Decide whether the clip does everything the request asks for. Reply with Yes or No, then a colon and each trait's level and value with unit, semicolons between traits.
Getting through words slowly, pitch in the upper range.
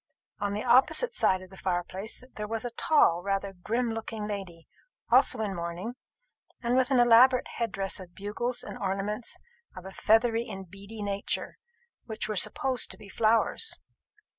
No: average, 165 wpm; high, 210 Hz